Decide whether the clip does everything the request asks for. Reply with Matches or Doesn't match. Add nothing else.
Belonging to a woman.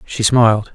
Doesn't match